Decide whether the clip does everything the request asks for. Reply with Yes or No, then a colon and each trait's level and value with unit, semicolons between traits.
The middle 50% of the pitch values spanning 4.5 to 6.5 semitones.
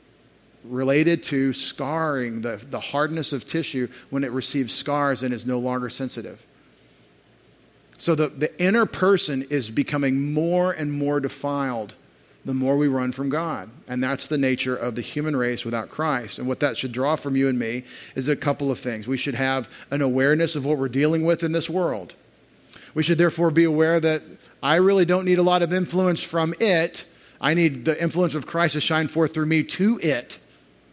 No: average, 3.7 semitones